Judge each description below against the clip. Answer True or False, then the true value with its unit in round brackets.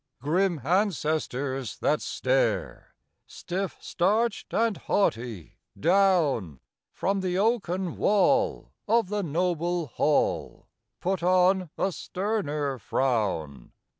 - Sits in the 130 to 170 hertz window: False (180 Hz)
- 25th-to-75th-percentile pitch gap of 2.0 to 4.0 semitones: False (5.6 semitones)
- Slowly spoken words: True (95 wpm)